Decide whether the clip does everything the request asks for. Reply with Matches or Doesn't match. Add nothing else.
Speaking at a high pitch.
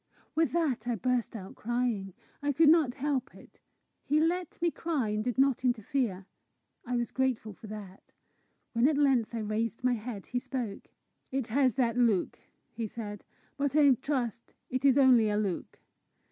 Matches